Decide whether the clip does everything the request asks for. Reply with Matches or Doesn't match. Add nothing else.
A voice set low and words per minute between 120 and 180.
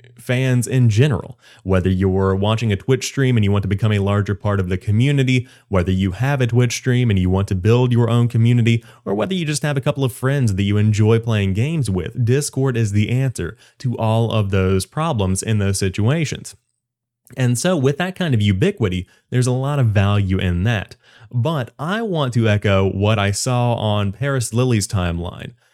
Doesn't match